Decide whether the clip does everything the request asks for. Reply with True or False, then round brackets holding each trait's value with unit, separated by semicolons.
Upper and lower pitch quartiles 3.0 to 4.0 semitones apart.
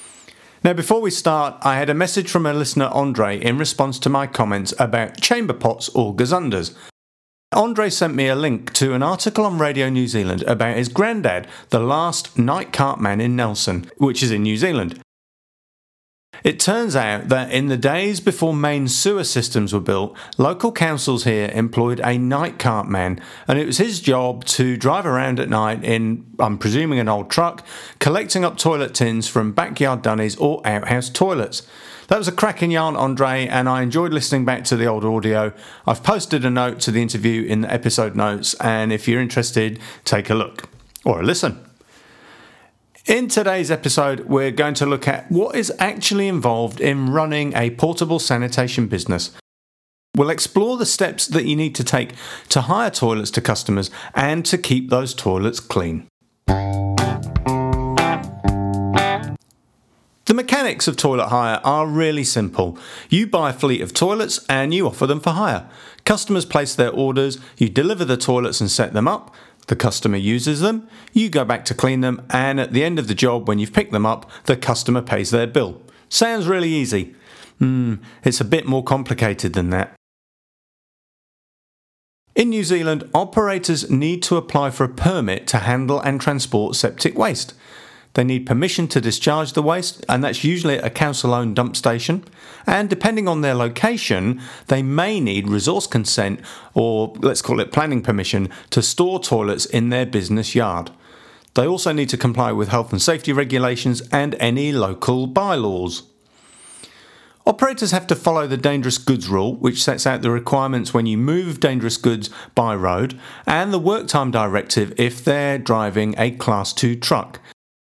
False (5.5 semitones)